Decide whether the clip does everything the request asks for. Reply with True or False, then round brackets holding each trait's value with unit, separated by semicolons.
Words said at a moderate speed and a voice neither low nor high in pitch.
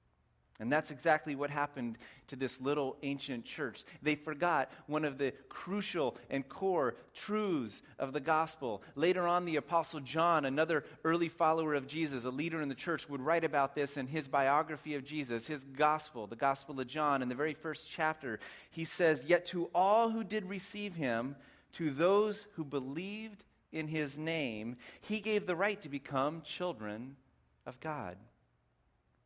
True (170 wpm; 155 Hz)